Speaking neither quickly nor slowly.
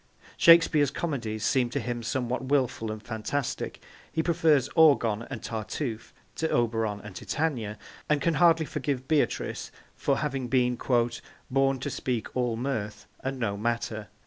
Yes: average, 145 wpm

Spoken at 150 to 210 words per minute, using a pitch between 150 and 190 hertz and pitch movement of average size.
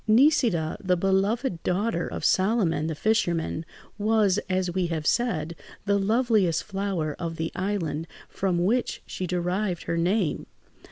No: slow, 135 wpm; medium, 185 Hz; average, 4.0 semitones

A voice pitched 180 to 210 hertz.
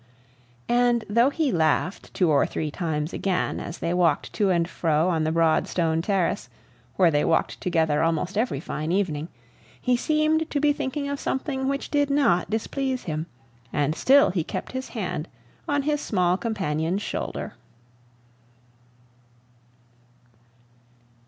Yes: medium, 185 Hz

